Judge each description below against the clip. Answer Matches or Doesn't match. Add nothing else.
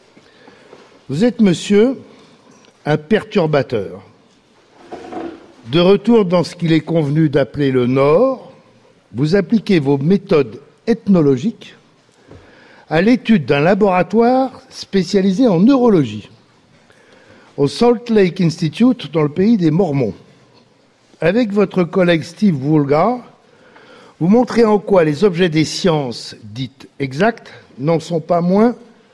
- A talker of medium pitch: Doesn't match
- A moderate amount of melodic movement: Doesn't match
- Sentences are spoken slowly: Matches